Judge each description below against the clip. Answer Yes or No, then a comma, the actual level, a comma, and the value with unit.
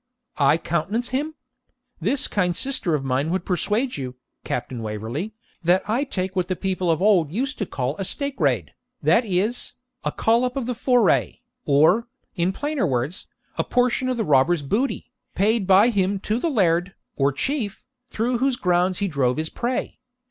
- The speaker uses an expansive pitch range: Yes, wide, 7.3 semitones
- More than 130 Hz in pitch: Yes, high, 190 Hz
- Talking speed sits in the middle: Yes, average, 170 wpm